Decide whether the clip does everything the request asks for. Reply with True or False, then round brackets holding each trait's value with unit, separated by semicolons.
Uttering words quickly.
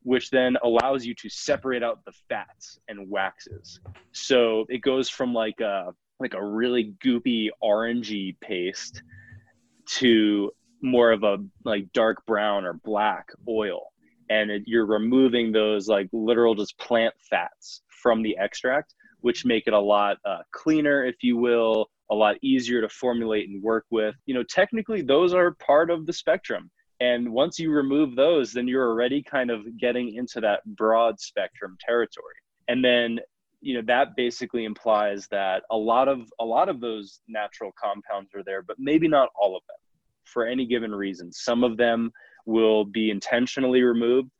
False (170 wpm)